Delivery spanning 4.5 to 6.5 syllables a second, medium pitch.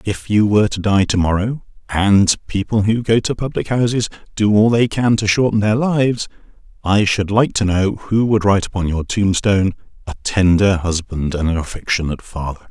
No: 5.3 syllables/s; low, 100 Hz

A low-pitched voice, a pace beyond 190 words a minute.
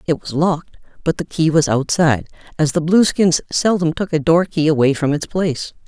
No: medium, 160 Hz; fast, 205 wpm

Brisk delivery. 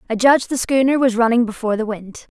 Yes: fast, 230 wpm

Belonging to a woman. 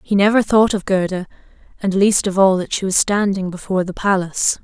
Yes: female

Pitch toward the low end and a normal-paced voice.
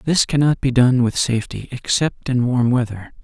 Yes: low, 125 Hz; average, 185 wpm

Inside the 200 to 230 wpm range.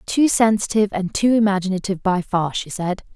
No: average, 170 wpm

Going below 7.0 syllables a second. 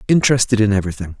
No: 8.7 syllables/s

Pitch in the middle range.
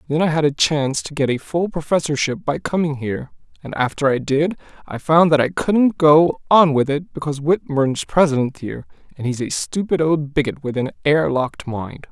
Yes: medium, 145 Hz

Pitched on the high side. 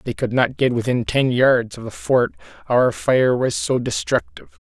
No: low, 125 Hz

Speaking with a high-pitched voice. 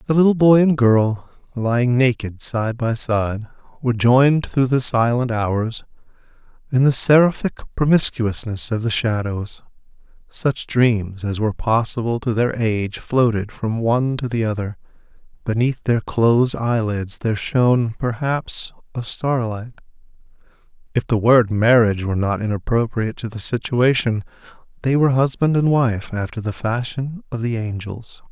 No: low, 120 Hz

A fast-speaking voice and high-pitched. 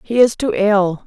Yes: fast, 225 wpm; high, 210 Hz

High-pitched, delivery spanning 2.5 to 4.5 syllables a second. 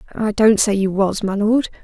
No: high, 210 Hz; 4.9 syllables/s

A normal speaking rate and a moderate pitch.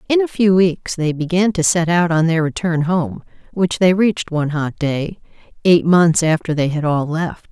No: fast, 210 wpm; medium, 170 Hz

